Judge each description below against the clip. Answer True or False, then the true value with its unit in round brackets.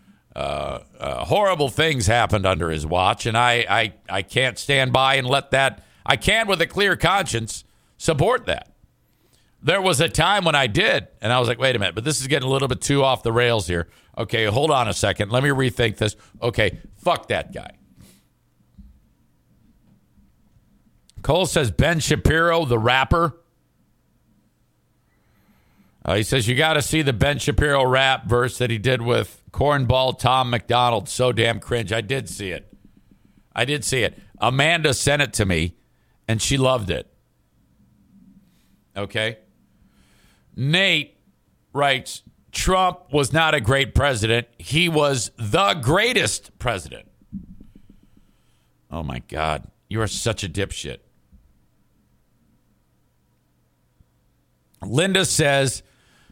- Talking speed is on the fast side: False (145 wpm)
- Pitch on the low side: True (120 Hz)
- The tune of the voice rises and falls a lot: True (6.1 semitones)